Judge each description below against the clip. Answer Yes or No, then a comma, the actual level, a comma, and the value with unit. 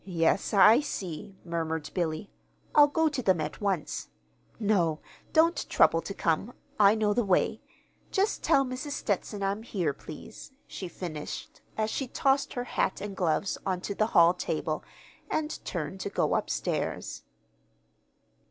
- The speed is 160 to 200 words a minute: No, average, 150 wpm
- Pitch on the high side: Yes, high, 200 Hz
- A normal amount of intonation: No, wide, 6.1 semitones